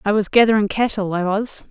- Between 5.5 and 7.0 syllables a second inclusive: Yes, 5.7 syllables/s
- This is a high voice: Yes, high, 205 Hz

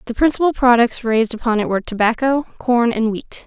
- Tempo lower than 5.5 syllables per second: No, 6.0 syllables/s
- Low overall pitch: No, high, 240 Hz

